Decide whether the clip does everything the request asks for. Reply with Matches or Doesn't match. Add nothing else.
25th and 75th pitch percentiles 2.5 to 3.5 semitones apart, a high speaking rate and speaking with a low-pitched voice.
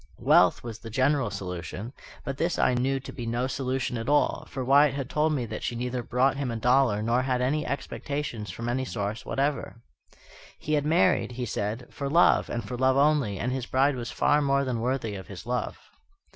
Matches